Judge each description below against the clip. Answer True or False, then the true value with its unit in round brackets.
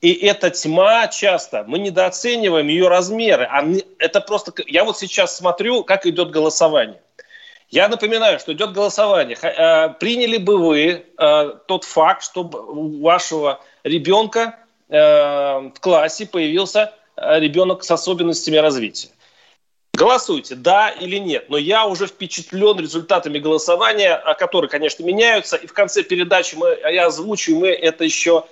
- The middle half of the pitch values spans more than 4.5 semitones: True (5.0 semitones)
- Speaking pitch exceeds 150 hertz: True (185 Hz)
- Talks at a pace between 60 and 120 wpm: False (130 wpm)